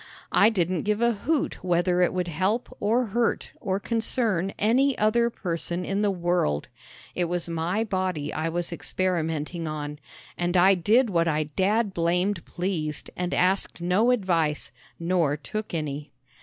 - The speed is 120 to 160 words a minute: Yes, average, 155 wpm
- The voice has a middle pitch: Yes, medium, 180 Hz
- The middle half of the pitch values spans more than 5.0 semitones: No, average, 3.8 semitones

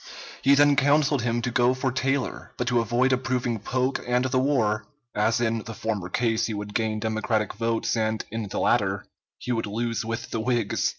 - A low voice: Yes, low, 115 Hz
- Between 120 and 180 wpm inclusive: No, average, 195 wpm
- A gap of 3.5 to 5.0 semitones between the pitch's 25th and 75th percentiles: No, narrow, 2.5 semitones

